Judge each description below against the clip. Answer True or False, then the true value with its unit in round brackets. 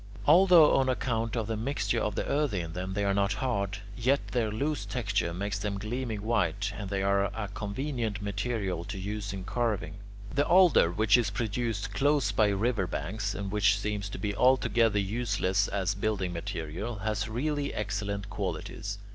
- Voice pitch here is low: True (105 Hz)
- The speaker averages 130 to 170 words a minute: False (180 wpm)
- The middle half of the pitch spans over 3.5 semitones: False (3.1 semitones)